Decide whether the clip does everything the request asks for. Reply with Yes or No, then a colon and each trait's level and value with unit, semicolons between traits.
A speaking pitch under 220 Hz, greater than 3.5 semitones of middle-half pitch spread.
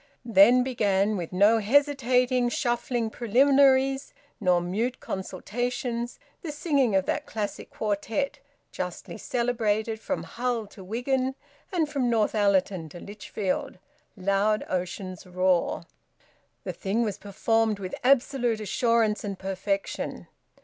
No: high, 225 Hz; average, 4.1 semitones